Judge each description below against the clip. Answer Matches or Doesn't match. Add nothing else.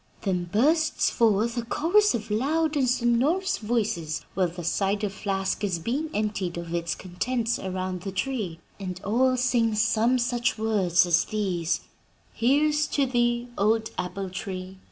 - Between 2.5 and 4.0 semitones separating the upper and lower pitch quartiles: Doesn't match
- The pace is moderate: Matches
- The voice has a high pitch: Matches